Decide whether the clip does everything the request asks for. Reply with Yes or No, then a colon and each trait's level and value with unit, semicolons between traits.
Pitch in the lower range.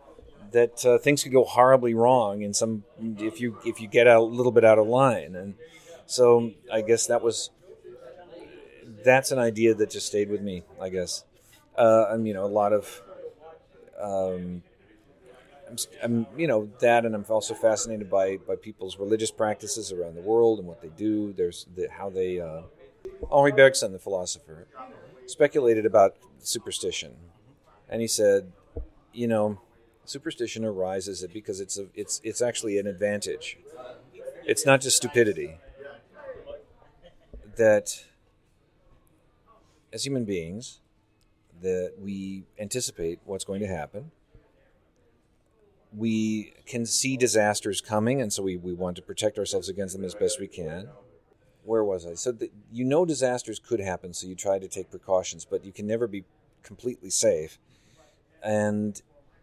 Yes: low, 110 Hz